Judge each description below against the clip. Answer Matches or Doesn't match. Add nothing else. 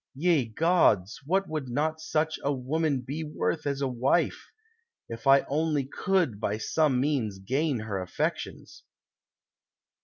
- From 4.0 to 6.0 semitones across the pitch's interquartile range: Matches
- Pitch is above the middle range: Doesn't match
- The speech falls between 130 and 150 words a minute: Matches